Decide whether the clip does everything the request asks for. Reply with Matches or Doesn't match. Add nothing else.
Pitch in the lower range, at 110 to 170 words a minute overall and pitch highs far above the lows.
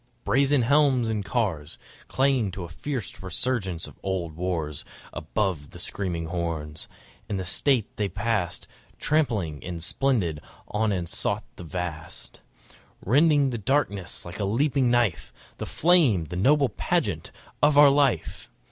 Matches